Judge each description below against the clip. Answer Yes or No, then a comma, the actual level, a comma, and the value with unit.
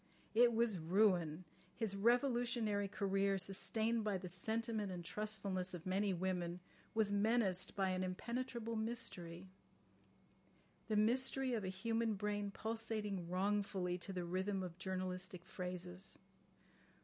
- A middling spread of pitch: Yes, average, 3.3 semitones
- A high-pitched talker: Yes, high, 200 Hz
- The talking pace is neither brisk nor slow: No, slow, 120 wpm